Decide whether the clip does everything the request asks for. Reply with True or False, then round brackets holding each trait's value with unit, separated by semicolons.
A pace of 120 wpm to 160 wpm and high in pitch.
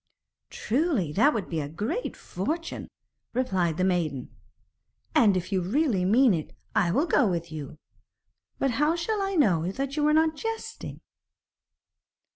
True (150 wpm; 215 Hz)